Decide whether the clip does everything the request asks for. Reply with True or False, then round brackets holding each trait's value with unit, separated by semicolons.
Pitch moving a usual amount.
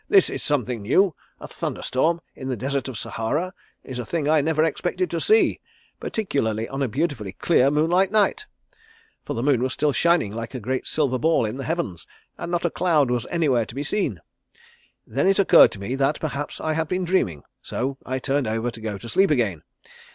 False (5.7 semitones)